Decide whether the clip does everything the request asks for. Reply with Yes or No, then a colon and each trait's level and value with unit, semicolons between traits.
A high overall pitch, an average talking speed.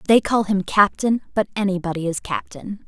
Yes: high, 200 Hz; average, 165 wpm